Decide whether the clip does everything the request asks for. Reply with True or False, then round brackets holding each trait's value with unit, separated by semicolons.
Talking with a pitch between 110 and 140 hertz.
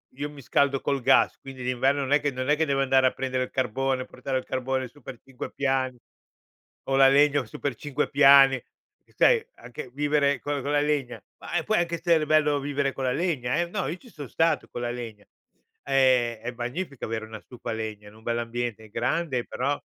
True (135 Hz)